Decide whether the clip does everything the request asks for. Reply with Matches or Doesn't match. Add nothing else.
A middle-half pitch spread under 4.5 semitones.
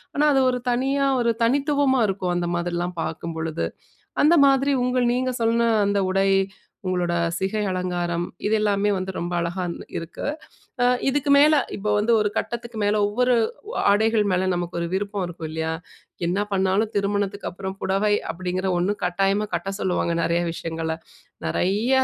Doesn't match